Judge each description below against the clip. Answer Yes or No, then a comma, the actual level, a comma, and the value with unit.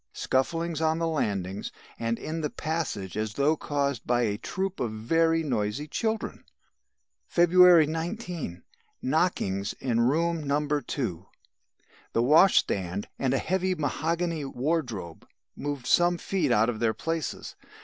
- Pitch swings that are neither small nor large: No, wide, 6.3 semitones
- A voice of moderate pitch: Yes, medium, 145 Hz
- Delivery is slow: Yes, slow, 130 wpm